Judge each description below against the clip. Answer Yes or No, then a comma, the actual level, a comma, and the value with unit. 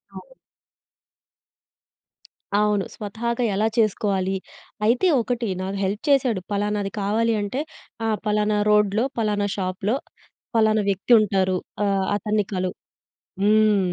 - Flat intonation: Yes, narrow, 1.9 semitones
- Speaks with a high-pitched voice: Yes, high, 210 Hz